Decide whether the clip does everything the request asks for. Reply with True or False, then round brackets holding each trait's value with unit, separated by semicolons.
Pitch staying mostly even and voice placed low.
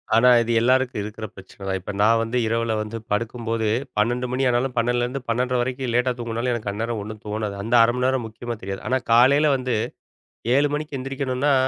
True (2.2 semitones; 120 Hz)